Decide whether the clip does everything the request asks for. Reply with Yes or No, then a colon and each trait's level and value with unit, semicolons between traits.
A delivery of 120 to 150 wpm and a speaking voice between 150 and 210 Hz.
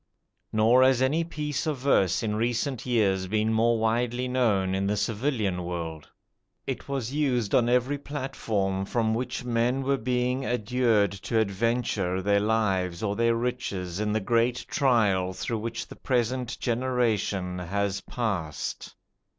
No: average, 145 wpm; low, 115 Hz